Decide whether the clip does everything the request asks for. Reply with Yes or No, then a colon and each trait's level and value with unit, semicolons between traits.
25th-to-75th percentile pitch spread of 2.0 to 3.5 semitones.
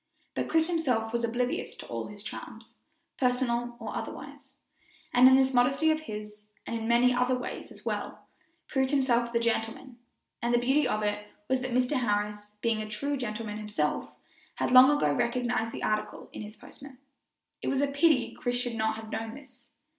Yes: average, 2.8 semitones